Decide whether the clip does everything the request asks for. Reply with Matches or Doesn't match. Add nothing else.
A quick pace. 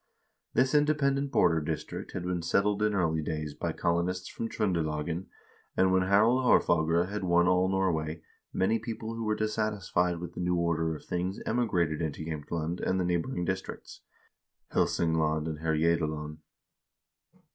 Doesn't match